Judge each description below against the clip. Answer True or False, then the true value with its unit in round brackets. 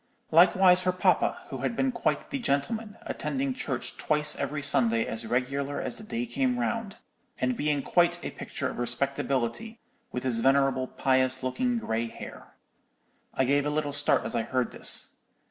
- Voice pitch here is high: False (145 Hz)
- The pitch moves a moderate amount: False (8.5 semitones)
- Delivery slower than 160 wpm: False (170 wpm)